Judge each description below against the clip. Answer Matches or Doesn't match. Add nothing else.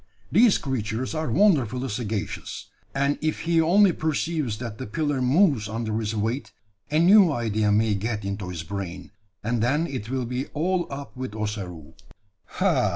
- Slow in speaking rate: Doesn't match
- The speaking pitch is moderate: Doesn't match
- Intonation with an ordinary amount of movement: Doesn't match